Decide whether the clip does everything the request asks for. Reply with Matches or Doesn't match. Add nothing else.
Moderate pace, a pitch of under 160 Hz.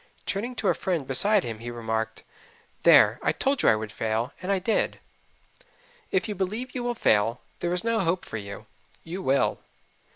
Doesn't match